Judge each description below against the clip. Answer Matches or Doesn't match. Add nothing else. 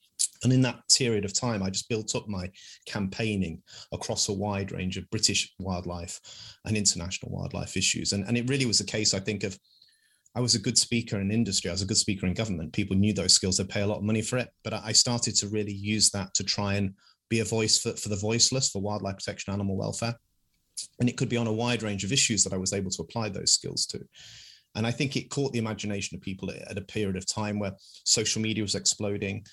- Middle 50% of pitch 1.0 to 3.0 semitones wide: Matches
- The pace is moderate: Doesn't match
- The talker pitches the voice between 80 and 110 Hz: Matches